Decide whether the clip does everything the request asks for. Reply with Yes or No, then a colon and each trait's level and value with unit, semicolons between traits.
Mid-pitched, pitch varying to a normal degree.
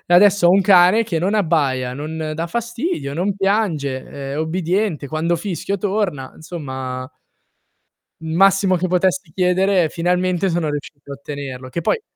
Yes: medium, 175 Hz; average, 4.4 semitones